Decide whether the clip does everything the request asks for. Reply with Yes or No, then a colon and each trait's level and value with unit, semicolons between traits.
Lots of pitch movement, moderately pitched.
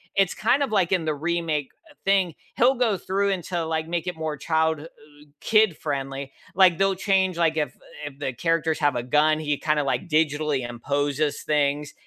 No: average, 4.0 semitones; medium, 160 Hz